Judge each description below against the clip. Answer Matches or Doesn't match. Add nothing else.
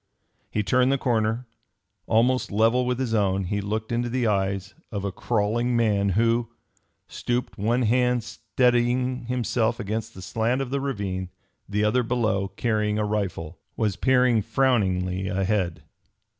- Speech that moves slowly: Doesn't match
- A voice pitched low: Matches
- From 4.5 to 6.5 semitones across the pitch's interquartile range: Doesn't match